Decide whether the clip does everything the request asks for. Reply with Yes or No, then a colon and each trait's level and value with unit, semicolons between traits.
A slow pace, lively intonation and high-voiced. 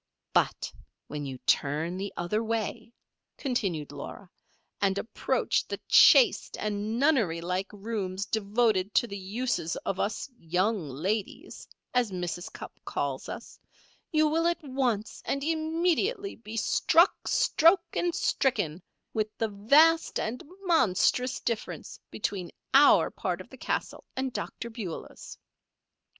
Yes: slow, 130 wpm; wide, 6.4 semitones; high, 220 Hz